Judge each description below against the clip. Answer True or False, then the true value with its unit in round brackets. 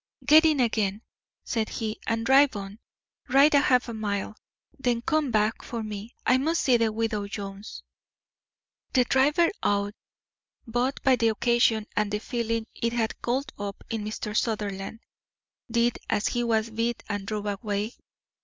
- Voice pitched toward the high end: True (225 Hz)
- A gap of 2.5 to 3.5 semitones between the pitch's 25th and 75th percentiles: True (2.8 semitones)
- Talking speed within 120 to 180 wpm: True (155 wpm)